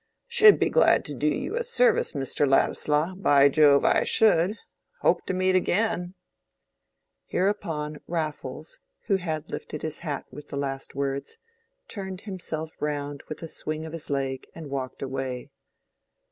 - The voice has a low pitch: No, medium, 155 Hz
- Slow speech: No, average, 145 wpm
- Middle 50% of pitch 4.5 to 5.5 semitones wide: Yes, average, 4.9 semitones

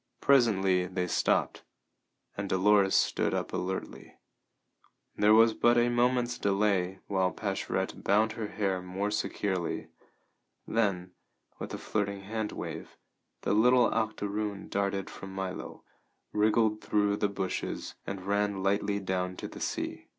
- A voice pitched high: No, low, 100 Hz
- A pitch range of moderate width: No, narrow, 2.2 semitones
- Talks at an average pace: No, slow, 130 wpm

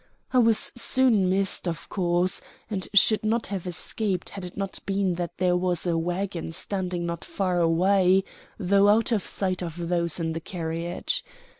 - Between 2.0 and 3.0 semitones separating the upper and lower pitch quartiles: Yes, narrow, 2.5 semitones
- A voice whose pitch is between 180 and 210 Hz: Yes, medium, 185 Hz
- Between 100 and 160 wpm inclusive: No, average, 170 wpm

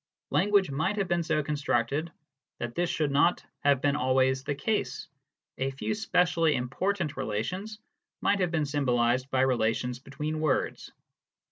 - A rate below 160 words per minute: Yes, average, 150 wpm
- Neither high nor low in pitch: Yes, medium, 145 Hz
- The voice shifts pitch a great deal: No, average, 4.8 semitones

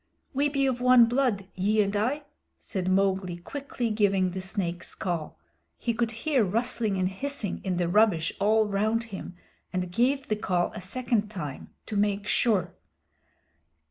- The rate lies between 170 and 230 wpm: No, average, 160 wpm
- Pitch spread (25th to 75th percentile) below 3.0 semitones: No, average, 4.2 semitones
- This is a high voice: Yes, high, 210 Hz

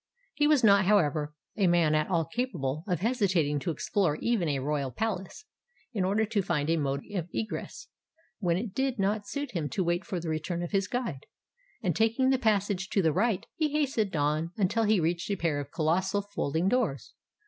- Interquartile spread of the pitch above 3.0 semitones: Yes, wide, 5.4 semitones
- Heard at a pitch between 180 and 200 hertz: Yes, medium, 185 Hz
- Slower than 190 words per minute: No, average, 200 wpm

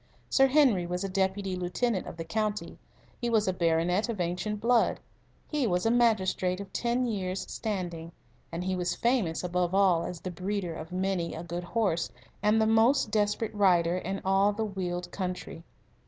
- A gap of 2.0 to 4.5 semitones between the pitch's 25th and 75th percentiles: Yes, average, 3.5 semitones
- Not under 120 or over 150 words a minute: No, average, 180 wpm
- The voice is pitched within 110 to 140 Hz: No, high, 190 Hz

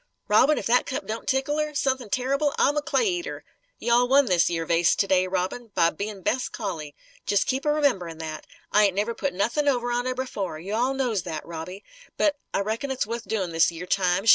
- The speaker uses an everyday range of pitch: No, wide, 6.6 semitones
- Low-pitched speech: No, high, 225 Hz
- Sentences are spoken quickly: Yes, fast, 225 wpm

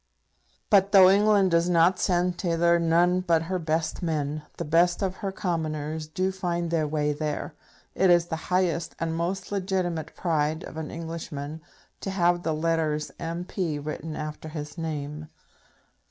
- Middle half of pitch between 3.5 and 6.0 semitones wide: No, narrow, 2.5 semitones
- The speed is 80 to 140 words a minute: No, average, 155 wpm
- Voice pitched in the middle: Yes, medium, 165 Hz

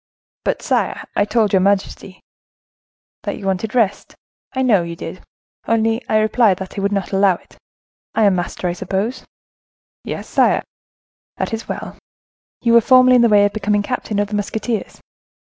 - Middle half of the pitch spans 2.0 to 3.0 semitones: Yes, average, 2.7 semitones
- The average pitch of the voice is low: No, high, 205 Hz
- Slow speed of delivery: No, average, 170 wpm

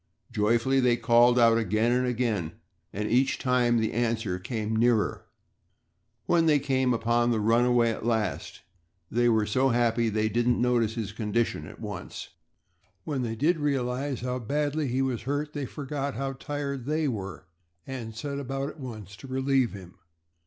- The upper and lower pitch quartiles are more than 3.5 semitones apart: No, average, 3.1 semitones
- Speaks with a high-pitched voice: No, low, 120 Hz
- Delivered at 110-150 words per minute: No, average, 165 wpm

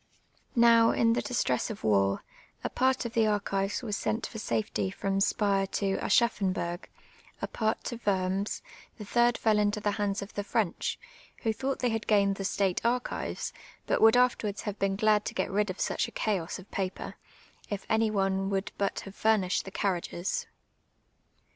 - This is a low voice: No, high, 205 Hz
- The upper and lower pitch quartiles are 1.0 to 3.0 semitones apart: Yes, narrow, 2.4 semitones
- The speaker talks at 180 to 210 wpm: Yes, average, 185 wpm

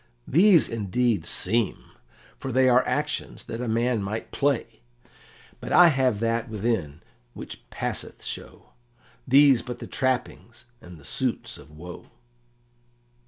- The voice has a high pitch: No, low, 120 Hz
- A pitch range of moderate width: Yes, average, 3.6 semitones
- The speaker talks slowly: Yes, slow, 130 wpm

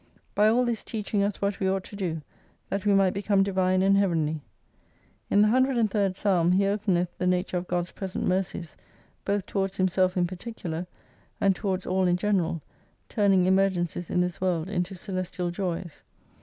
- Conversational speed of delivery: Yes, average, 170 wpm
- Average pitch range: No, narrow, 1.9 semitones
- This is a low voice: No, high, 190 Hz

